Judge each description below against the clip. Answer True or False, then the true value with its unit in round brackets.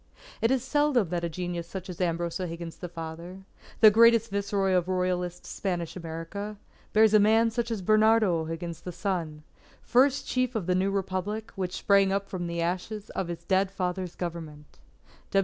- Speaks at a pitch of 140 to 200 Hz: True (185 Hz)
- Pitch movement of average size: True (3.6 semitones)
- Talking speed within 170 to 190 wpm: True (175 wpm)